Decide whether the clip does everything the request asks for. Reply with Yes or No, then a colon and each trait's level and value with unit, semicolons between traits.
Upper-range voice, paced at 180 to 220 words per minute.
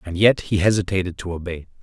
No: very low, 95 Hz; average, 200 wpm